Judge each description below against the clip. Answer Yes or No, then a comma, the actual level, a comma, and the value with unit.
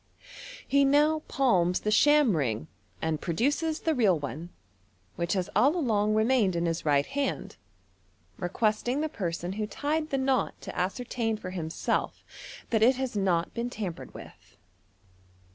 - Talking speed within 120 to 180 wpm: Yes, average, 150 wpm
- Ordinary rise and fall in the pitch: No, wide, 7.5 semitones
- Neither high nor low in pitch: No, high, 215 Hz